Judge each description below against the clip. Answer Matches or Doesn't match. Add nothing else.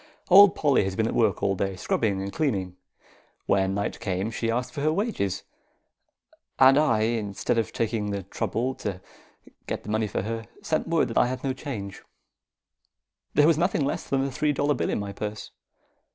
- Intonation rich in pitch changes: Matches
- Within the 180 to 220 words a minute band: Matches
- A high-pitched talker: Doesn't match